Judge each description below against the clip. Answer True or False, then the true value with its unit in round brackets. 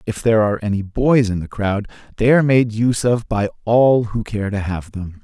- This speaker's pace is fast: True (230 wpm)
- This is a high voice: False (110 Hz)